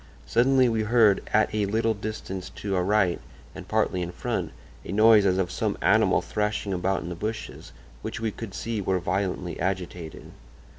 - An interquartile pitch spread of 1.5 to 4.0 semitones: Yes, average, 2.9 semitones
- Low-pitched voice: Yes, low, 100 Hz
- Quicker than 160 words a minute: Yes, average, 180 wpm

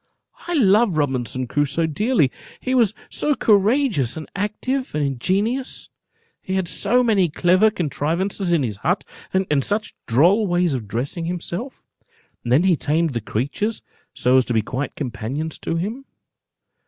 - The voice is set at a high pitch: No, medium, 175 Hz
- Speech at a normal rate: Yes, average, 155 wpm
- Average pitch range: No, wide, 7.2 semitones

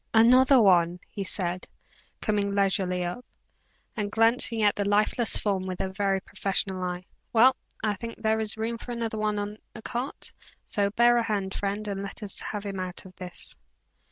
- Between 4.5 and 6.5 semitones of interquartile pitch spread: No, narrow, 2.6 semitones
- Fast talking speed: No, average, 185 wpm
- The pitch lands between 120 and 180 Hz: No, high, 205 Hz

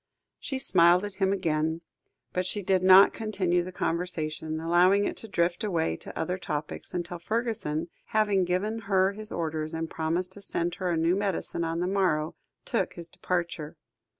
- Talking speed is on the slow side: No, average, 175 wpm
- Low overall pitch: No, medium, 180 Hz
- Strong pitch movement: No, average, 3.0 semitones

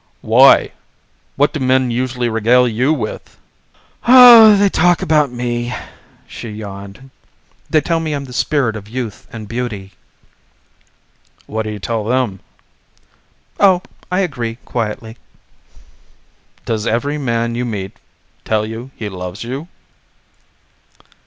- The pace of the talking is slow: Yes, slow, 125 wpm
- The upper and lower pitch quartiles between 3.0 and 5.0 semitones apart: Yes, average, 4.5 semitones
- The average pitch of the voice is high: No, low, 120 Hz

